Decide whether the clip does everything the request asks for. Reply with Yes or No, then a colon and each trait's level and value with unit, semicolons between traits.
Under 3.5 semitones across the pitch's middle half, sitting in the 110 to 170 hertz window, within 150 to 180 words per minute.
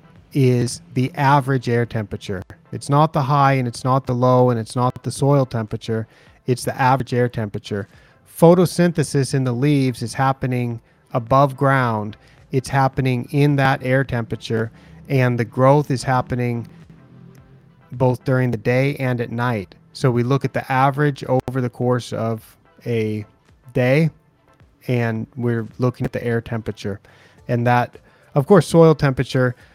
Yes: narrow, 2.4 semitones; low, 130 Hz; average, 155 wpm